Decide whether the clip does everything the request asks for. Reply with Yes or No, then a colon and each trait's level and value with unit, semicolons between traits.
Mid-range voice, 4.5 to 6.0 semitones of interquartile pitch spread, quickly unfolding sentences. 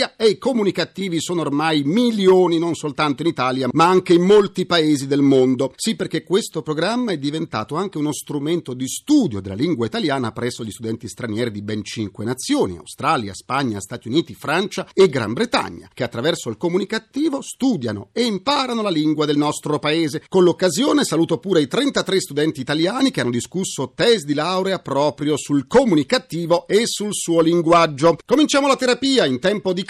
Yes: medium, 165 Hz; wide, 5.4 semitones; fast, 175 wpm